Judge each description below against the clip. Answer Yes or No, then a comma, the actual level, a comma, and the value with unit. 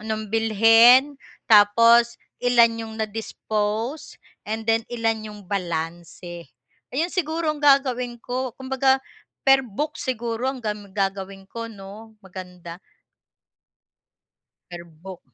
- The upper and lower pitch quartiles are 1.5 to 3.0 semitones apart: No, average, 4.0 semitones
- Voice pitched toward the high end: Yes, high, 225 Hz